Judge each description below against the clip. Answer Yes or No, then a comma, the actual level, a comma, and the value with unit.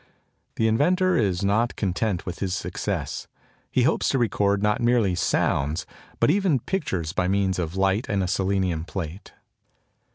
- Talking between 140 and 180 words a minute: Yes, average, 155 wpm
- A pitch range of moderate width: Yes, average, 3.8 semitones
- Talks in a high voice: No, low, 100 Hz